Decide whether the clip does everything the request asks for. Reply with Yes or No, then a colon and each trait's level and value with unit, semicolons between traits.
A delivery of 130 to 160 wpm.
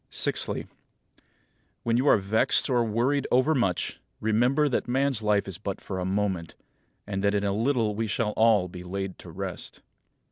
No: average, 170 wpm